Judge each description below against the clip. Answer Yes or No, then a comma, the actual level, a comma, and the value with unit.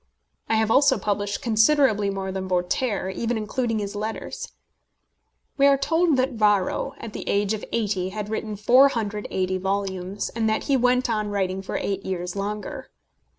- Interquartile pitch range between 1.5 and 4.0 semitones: Yes, average, 3.4 semitones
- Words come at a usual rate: Yes, average, 160 wpm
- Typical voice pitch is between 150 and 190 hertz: No, high, 210 Hz